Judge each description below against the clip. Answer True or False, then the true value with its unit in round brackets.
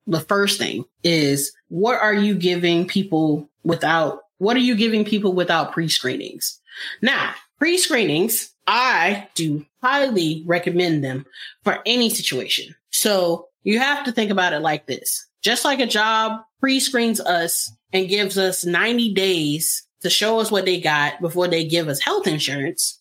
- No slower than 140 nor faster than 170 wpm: True (160 wpm)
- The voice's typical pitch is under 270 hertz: True (185 Hz)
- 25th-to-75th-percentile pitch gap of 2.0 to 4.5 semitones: False (4.9 semitones)